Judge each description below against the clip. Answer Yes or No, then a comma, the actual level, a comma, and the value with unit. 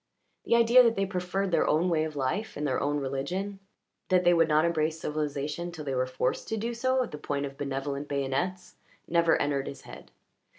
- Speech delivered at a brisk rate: Yes, fast, 210 wpm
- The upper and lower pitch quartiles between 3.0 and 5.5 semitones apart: Yes, average, 4.7 semitones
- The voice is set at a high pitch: No, medium, 155 Hz